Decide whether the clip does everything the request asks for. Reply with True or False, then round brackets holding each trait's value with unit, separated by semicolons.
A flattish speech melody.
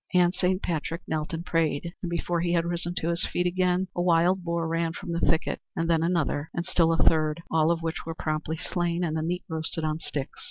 True (1.4 semitones)